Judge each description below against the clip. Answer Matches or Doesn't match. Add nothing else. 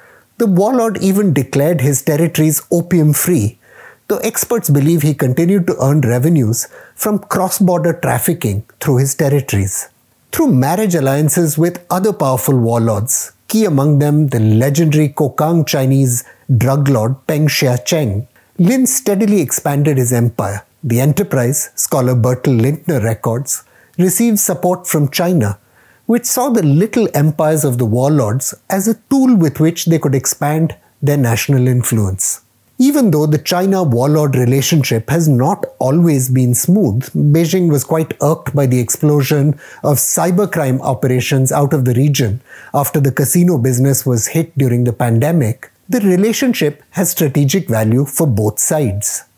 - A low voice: Doesn't match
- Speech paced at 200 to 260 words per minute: Doesn't match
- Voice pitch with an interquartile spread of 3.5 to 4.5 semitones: Doesn't match